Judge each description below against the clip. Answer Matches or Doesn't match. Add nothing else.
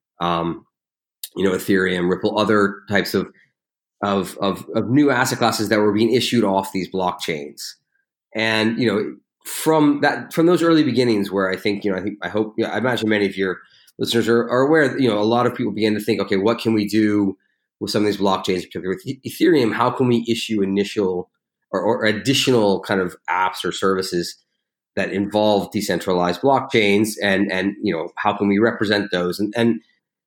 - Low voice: Matches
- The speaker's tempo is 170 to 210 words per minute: Matches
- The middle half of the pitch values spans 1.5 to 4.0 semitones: Matches